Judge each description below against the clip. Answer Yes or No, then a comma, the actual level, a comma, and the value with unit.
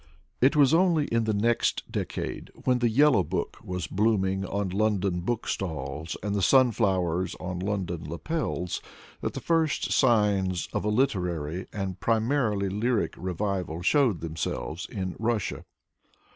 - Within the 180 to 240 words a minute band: No, slow, 135 wpm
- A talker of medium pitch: No, low, 100 Hz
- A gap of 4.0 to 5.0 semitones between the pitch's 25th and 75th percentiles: Yes, average, 4.6 semitones